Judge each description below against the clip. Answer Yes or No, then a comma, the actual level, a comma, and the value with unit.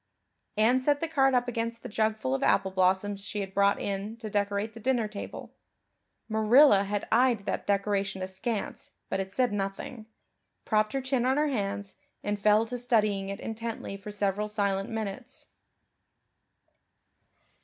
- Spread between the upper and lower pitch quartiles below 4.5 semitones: Yes, average, 2.8 semitones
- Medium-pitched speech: No, high, 210 Hz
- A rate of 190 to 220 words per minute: No, average, 155 wpm